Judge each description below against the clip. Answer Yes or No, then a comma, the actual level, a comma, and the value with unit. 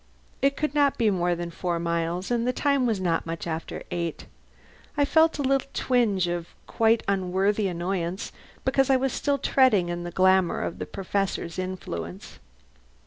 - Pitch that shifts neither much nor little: No, wide, 6.6 semitones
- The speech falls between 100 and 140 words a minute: No, average, 170 wpm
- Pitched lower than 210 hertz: Yes, high, 190 Hz